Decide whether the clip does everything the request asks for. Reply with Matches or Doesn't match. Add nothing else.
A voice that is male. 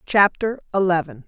Doesn't match